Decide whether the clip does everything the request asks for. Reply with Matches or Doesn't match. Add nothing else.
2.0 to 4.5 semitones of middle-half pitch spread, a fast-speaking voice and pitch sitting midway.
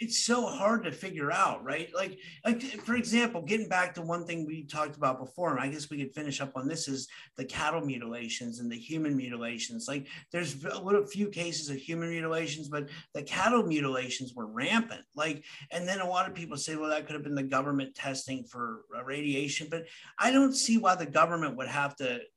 Doesn't match